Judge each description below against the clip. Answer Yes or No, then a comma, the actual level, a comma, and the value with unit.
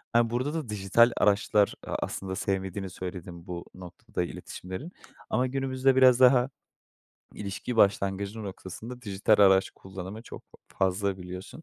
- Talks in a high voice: No, low, 100 Hz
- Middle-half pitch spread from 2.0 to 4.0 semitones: No, average, 4.5 semitones